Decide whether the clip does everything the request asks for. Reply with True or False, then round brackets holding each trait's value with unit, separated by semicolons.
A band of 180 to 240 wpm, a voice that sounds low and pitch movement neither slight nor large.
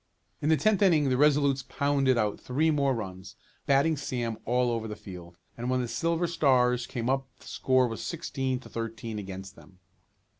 True (185 wpm; 125 Hz; 3.9 semitones)